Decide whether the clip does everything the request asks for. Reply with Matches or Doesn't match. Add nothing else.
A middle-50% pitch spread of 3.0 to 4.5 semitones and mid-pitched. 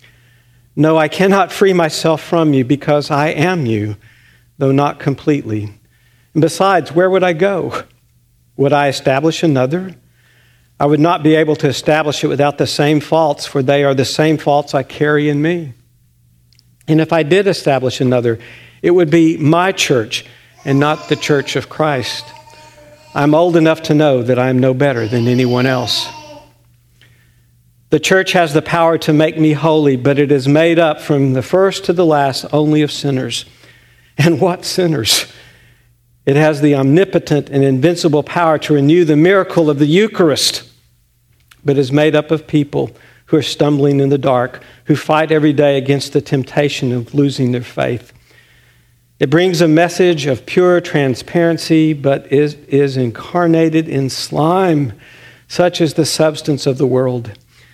Matches